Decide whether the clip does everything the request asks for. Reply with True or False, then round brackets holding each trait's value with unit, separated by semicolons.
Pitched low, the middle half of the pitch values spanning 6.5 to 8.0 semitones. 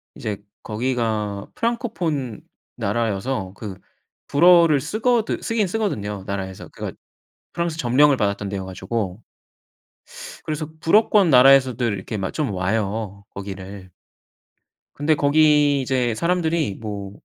True (120 Hz; 7.5 semitones)